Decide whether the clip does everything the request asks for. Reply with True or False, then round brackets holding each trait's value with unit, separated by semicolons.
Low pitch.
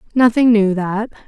False (215 Hz)